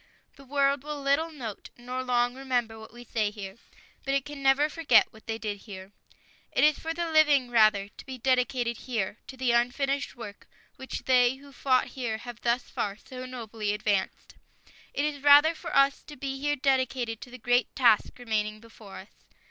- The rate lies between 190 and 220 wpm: Yes, average, 195 wpm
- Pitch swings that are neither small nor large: Yes, average, 3.7 semitones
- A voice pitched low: No, very high, 250 Hz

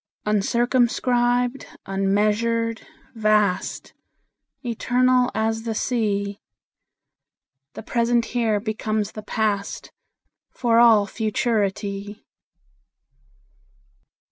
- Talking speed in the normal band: No, slow, 65 wpm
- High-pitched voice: Yes, high, 220 Hz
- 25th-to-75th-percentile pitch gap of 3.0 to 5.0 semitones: No, narrow, 2.5 semitones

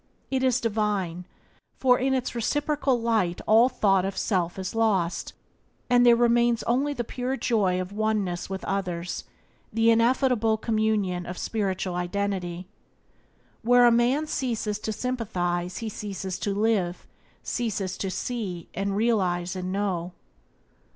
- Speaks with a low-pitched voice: No, high, 210 Hz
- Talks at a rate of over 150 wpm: No, slow, 135 wpm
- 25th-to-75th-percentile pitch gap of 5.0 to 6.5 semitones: No, average, 4.3 semitones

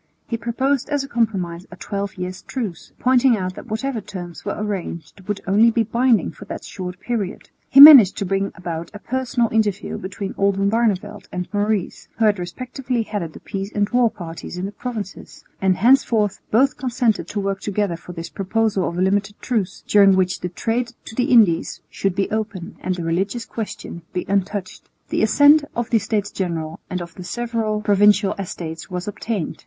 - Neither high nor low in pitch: No, high, 205 Hz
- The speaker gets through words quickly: No, average, 185 wpm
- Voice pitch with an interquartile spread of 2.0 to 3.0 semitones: No, average, 3.8 semitones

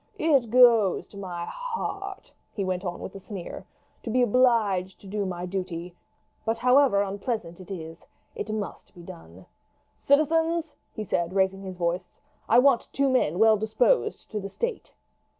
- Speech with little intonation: No, wide, 5.5 semitones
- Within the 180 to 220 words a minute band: No, average, 165 wpm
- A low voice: No, high, 205 Hz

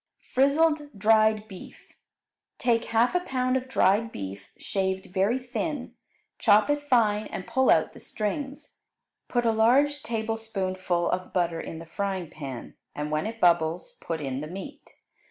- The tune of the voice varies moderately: No, wide, 5.9 semitones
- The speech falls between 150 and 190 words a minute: Yes, average, 155 wpm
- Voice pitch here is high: Yes, high, 215 Hz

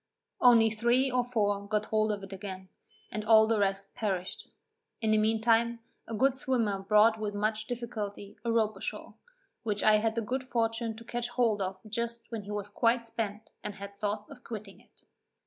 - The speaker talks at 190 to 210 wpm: Yes, average, 195 wpm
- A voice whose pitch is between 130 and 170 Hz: No, high, 220 Hz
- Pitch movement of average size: No, narrow, 2.2 semitones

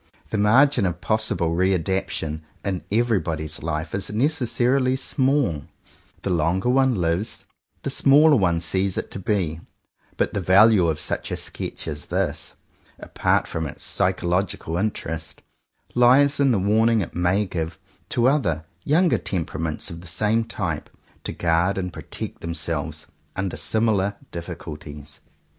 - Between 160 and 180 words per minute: No, average, 145 wpm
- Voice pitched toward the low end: Yes, very low, 95 Hz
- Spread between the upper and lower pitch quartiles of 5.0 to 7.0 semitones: Yes, wide, 5.6 semitones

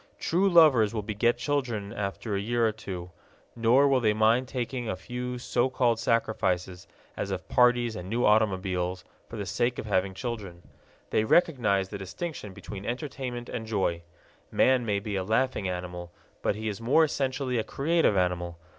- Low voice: Yes, low, 110 Hz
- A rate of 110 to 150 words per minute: No, average, 175 wpm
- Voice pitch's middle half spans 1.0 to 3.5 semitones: No, average, 4.1 semitones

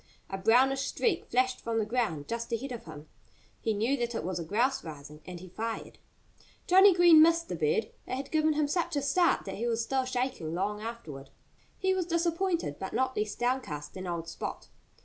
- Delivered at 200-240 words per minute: Yes, fast, 205 wpm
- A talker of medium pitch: No, high, 240 Hz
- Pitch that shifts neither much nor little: No, wide, 8.3 semitones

